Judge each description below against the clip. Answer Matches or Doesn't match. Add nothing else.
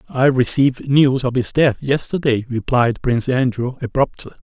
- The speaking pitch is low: Matches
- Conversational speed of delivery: Matches